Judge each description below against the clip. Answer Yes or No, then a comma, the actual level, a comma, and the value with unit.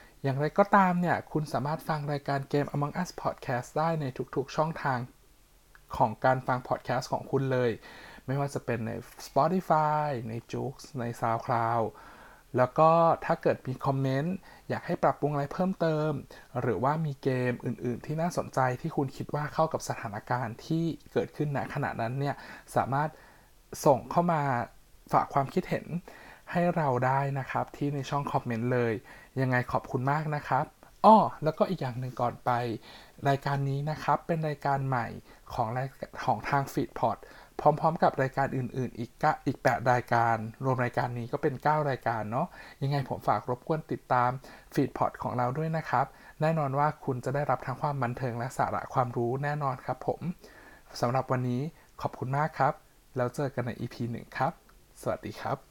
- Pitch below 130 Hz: No, low, 135 Hz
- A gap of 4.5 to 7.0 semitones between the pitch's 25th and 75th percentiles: No, average, 3.4 semitones